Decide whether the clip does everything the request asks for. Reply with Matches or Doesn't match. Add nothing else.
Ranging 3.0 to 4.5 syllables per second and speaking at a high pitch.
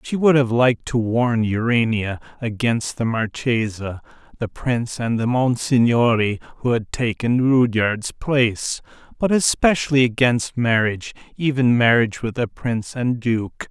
Doesn't match